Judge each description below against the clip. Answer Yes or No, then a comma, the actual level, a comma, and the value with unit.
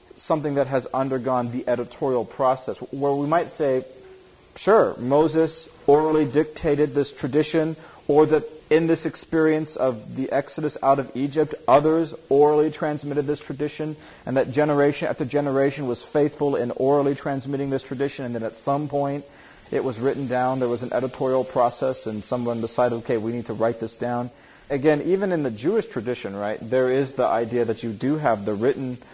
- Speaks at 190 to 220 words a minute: No, average, 175 wpm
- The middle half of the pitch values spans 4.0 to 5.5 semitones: No, average, 3.2 semitones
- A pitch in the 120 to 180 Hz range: Yes, medium, 140 Hz